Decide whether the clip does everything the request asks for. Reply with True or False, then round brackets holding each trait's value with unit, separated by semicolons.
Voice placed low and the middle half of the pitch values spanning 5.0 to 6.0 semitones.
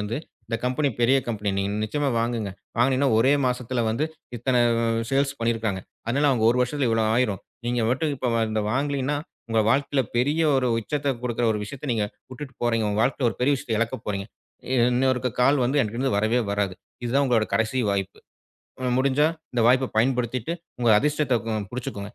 False (125 Hz; 3.1 semitones)